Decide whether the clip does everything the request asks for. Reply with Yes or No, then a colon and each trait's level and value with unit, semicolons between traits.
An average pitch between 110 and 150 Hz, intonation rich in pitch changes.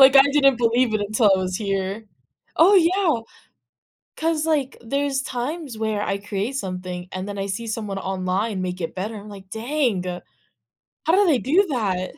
No: high, 220 Hz; wide, 5.9 semitones